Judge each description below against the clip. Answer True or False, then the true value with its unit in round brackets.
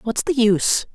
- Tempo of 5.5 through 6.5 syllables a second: False (4.7 syllables/s)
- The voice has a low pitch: False (230 Hz)